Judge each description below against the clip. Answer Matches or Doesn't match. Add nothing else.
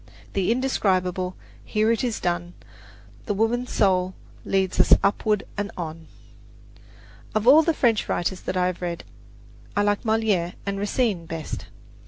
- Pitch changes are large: Doesn't match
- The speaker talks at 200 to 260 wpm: Doesn't match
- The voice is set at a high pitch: Matches